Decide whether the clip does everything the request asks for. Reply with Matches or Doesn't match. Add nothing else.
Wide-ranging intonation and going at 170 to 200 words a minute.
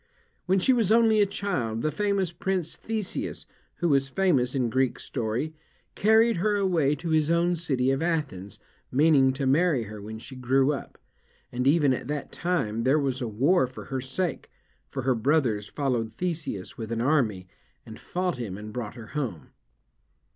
Matches